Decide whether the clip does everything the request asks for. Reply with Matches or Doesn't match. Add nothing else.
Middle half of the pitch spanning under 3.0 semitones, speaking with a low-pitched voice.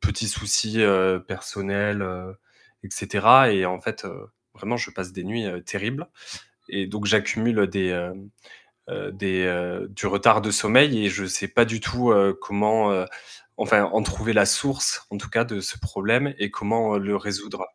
Matches